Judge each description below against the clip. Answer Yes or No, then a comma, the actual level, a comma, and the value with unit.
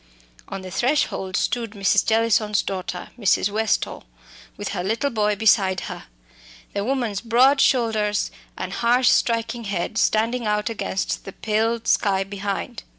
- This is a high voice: Yes, high, 215 Hz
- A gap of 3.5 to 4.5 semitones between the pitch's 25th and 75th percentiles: No, average, 2.7 semitones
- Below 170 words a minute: Yes, average, 140 wpm